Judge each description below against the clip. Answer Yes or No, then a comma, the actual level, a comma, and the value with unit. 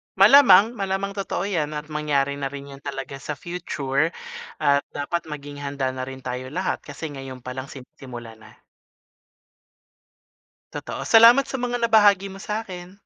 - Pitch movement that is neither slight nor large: No, wide, 6.2 semitones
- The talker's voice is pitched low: No, medium, 150 Hz